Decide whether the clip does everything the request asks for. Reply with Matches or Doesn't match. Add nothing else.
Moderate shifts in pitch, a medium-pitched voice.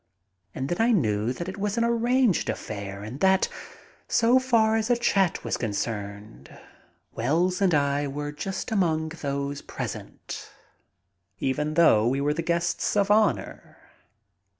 Doesn't match